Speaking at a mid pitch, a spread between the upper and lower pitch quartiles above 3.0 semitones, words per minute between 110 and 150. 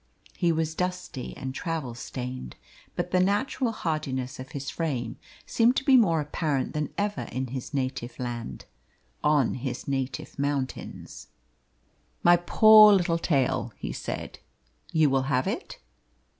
Yes: medium, 150 Hz; wide, 5.5 semitones; average, 140 wpm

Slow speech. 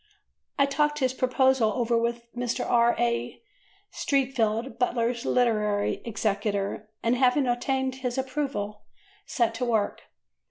Yes: slow, 120 wpm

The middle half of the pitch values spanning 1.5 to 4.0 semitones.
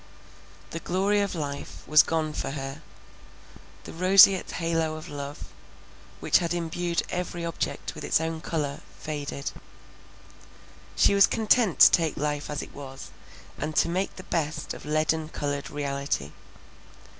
Yes: average, 2.9 semitones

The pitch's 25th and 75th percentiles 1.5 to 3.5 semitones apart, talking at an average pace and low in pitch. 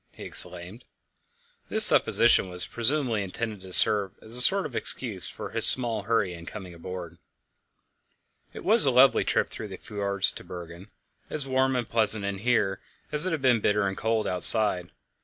No: average, 4.8 semitones; average, 180 wpm; low, 105 Hz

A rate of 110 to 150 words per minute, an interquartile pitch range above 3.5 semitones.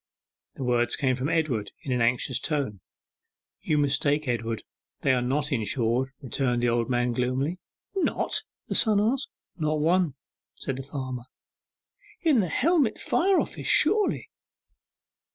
Yes: average, 140 wpm; average, 4.7 semitones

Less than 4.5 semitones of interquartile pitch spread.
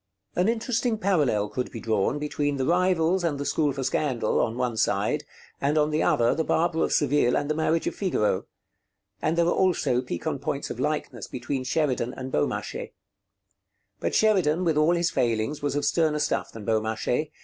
No: average, 4.8 semitones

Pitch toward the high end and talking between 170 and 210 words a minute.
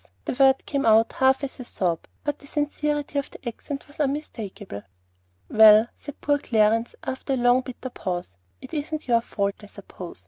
Yes: very high, 255 Hz; average, 180 wpm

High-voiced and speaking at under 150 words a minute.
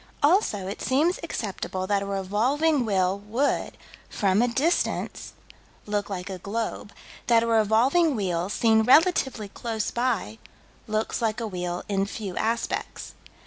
Yes: high, 220 Hz; average, 140 wpm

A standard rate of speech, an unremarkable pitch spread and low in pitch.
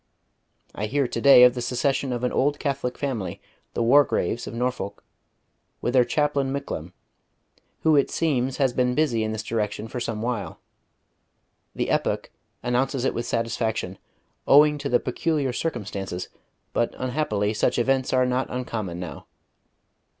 Yes: average, 150 wpm; average, 3.5 semitones; low, 125 Hz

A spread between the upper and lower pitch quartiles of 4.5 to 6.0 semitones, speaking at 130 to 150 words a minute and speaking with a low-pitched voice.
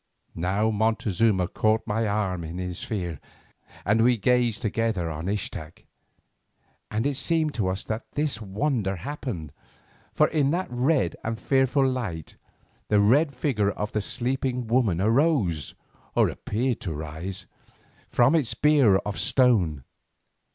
Yes: average, 5.3 semitones; slow, 135 wpm; low, 110 Hz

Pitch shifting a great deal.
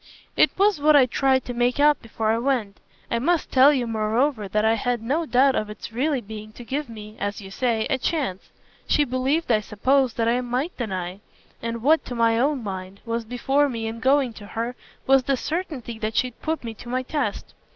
No: average, 3.7 semitones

